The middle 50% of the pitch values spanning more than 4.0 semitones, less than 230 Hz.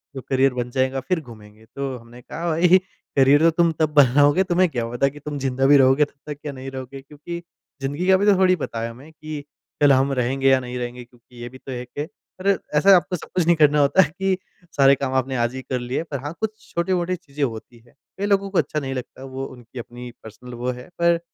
Yes: average, 4.6 semitones; low, 135 Hz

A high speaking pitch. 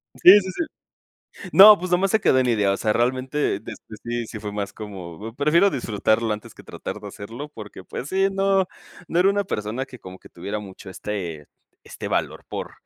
No: low, 120 Hz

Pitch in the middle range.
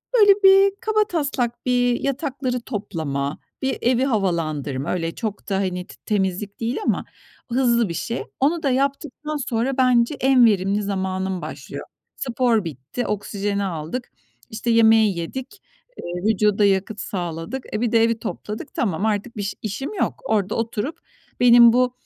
No: high, 225 Hz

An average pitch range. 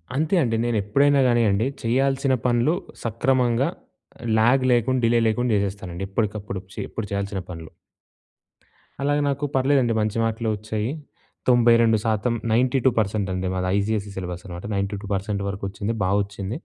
Yes: average, 3.7 semitones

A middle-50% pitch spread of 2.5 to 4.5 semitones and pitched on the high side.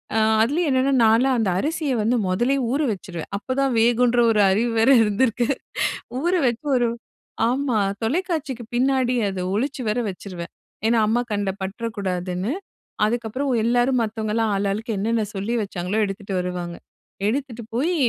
Yes: average, 4.2 semitones; high, 230 Hz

